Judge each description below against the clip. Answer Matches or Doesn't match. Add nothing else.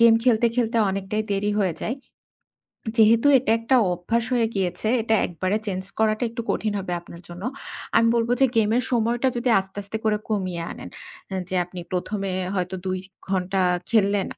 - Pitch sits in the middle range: Doesn't match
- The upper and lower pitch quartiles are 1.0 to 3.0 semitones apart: Doesn't match